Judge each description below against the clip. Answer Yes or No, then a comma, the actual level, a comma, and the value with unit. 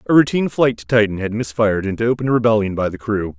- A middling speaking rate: No, fast, 230 wpm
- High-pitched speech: No, low, 110 Hz